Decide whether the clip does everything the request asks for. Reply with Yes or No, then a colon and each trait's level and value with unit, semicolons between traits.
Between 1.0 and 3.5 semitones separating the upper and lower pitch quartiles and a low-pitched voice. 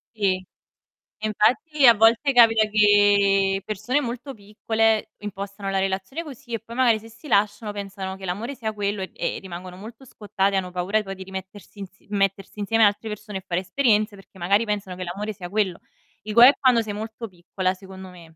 No: narrow, 2.6 semitones; high, 205 Hz